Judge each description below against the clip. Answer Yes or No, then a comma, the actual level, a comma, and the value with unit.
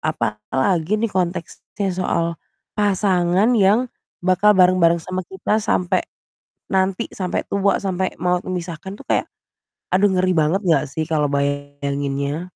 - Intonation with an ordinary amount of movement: Yes, average, 3.4 semitones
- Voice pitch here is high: No, medium, 180 Hz